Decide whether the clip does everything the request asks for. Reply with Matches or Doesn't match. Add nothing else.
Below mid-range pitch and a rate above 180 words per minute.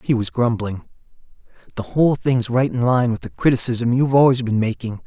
Matches